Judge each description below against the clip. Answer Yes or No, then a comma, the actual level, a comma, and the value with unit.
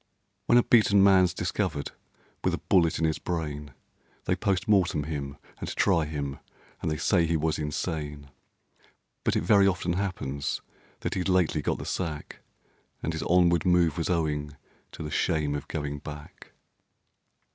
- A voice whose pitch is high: No, very low, 80 Hz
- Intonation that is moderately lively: Yes, average, 3.6 semitones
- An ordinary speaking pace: Yes, average, 160 wpm